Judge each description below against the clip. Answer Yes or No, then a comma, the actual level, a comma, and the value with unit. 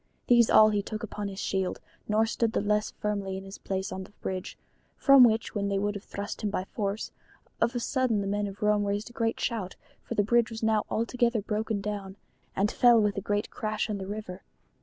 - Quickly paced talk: Yes, fast, 225 wpm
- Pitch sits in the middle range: No, high, 210 Hz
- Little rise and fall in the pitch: Yes, narrow, 2.0 semitones